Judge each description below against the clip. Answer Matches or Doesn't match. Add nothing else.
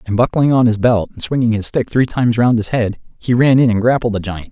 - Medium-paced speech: Doesn't match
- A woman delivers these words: Doesn't match